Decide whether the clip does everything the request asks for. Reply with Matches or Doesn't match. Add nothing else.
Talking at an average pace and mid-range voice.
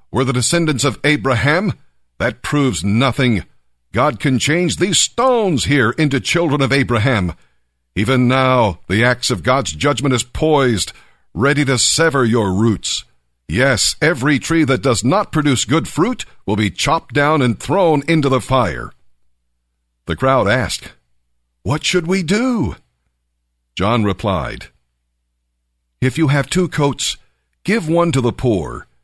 Doesn't match